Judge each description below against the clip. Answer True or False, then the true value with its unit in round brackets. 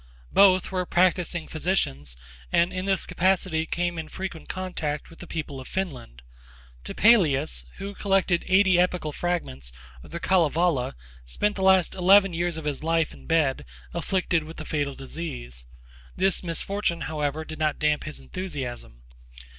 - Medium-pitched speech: True (165 Hz)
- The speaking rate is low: False (150 wpm)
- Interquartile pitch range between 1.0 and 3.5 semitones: False (3.9 semitones)